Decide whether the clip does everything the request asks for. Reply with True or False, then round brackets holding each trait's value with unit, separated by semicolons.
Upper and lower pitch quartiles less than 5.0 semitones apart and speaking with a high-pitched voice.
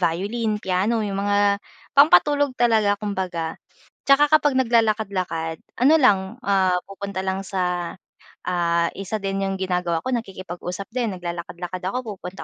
True (3.8 semitones; 195 Hz)